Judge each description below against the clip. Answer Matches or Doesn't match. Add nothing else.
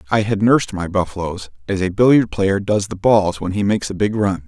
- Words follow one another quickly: Matches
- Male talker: Matches